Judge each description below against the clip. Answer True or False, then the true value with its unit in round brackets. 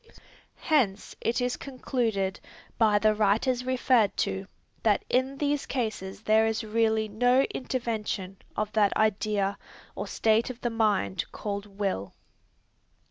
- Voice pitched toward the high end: True (220 Hz)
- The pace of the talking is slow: True (130 wpm)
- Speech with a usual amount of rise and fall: True (3.4 semitones)